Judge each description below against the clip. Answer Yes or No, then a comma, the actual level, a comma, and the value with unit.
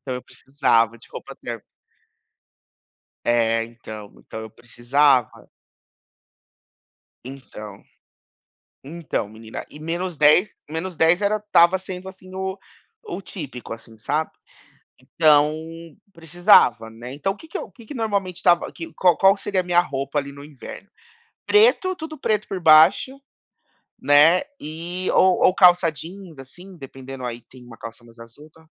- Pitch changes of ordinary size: No, wide, 6.8 semitones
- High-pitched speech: No, medium, 155 Hz